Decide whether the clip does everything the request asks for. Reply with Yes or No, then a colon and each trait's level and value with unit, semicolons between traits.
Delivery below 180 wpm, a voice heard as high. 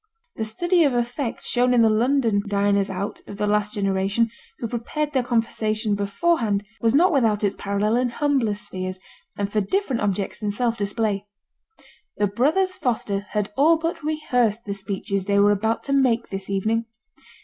Yes: average, 170 wpm; high, 220 Hz